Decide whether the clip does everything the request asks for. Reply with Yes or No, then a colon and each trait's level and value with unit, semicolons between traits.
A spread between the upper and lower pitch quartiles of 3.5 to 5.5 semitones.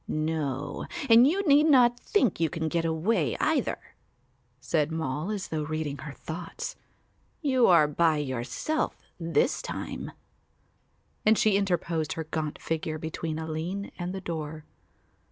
Yes: average, 4.4 semitones